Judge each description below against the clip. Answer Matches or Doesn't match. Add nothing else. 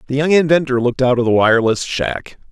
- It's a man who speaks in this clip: Matches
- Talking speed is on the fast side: Matches